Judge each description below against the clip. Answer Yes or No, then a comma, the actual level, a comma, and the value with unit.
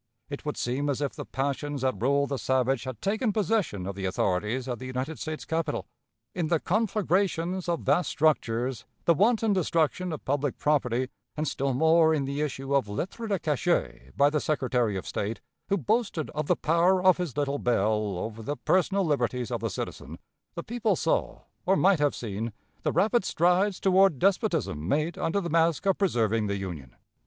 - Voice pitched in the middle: Yes, medium, 150 Hz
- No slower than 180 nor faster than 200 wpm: Yes, average, 185 wpm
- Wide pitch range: Yes, wide, 6.3 semitones